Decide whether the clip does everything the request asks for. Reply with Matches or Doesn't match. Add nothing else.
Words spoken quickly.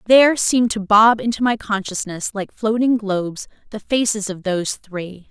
Doesn't match